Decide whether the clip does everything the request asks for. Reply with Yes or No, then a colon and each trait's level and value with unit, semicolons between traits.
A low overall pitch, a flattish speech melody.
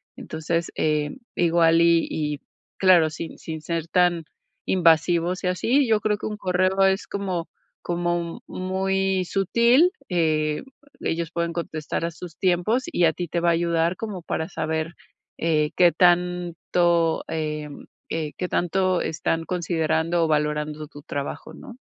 No: medium, 170 Hz; narrow, 2.3 semitones